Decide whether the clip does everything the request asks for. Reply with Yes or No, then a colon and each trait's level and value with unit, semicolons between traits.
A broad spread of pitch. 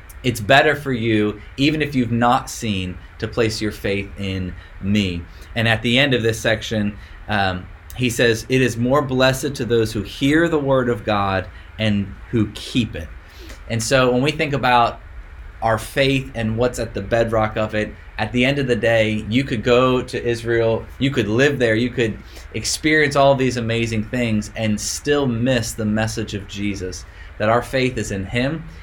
No: average, 3.7 semitones